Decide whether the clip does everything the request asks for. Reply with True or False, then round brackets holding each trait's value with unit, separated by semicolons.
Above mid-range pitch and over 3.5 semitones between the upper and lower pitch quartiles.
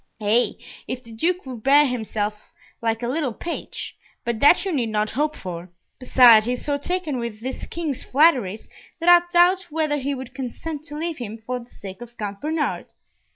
True (255 Hz; 5.4 semitones)